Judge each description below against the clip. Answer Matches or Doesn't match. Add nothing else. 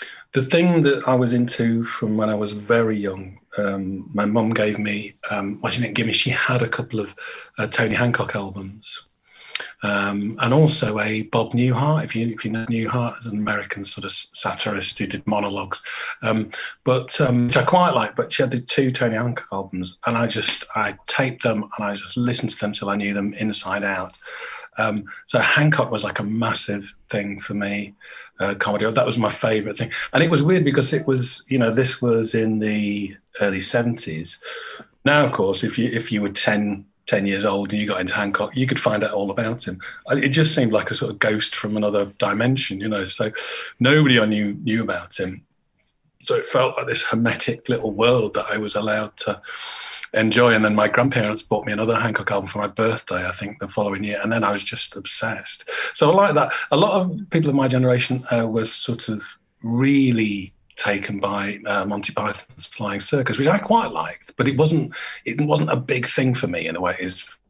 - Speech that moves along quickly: Matches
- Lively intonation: Doesn't match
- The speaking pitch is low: Matches